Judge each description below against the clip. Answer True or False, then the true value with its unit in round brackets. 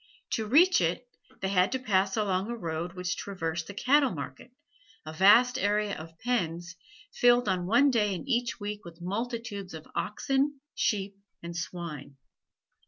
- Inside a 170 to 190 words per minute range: False (160 wpm)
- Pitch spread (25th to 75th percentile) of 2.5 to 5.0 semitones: False (5.5 semitones)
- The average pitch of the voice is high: True (200 Hz)